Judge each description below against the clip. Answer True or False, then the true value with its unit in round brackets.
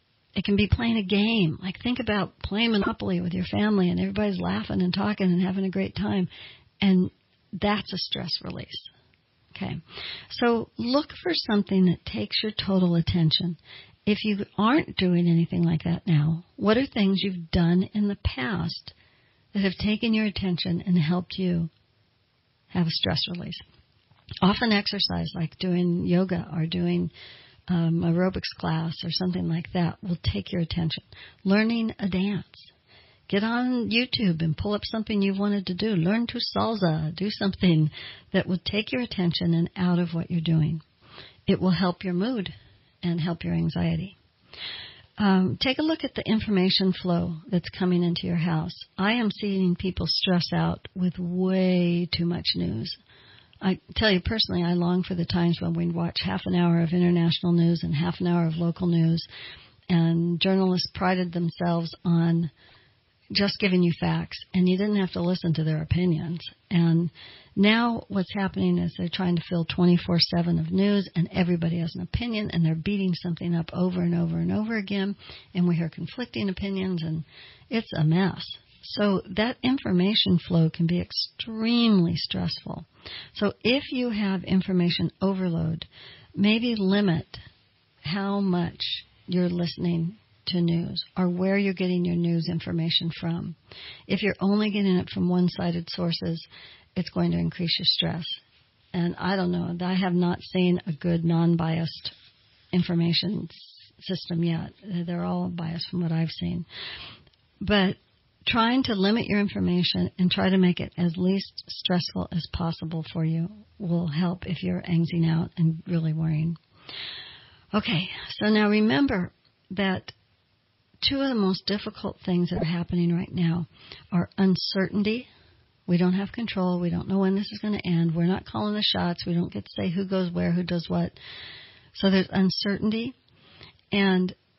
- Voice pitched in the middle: True (180 Hz)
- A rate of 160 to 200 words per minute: True (165 wpm)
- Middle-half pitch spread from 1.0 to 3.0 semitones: True (2.6 semitones)